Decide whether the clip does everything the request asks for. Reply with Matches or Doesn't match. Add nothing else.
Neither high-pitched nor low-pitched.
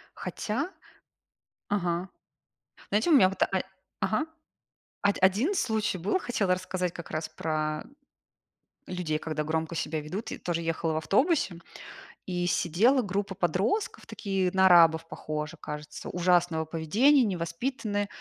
Matches